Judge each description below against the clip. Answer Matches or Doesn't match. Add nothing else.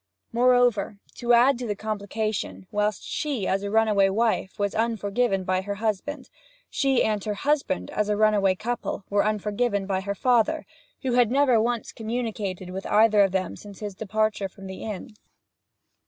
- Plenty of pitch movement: Doesn't match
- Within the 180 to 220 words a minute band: Doesn't match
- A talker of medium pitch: Doesn't match